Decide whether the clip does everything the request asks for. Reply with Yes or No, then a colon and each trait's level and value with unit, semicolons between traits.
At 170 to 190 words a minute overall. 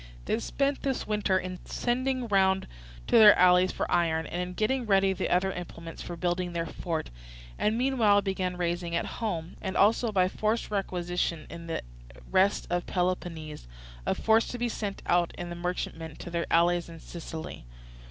Yes: average, 175 wpm